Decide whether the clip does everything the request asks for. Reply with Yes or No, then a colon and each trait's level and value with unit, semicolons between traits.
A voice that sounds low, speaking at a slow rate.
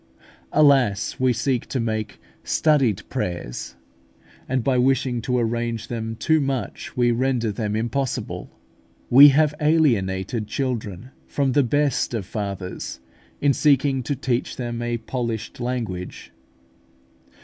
Yes: low, 120 Hz; slow, 125 wpm